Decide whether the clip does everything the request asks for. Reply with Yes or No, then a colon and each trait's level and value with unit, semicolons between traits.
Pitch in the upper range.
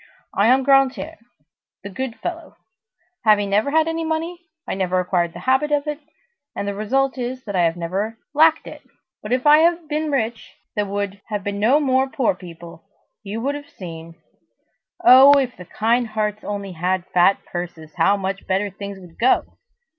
Yes: high, 215 Hz